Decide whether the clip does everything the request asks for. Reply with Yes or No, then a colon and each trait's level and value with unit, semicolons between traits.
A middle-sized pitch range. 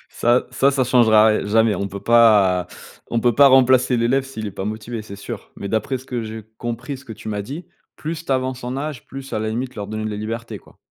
Yes: average, 3.2 semitones